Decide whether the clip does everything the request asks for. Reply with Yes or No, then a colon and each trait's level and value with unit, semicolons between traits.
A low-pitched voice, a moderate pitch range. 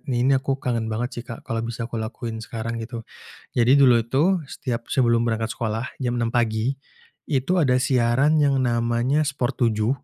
No: low, 120 Hz; narrow, 2.3 semitones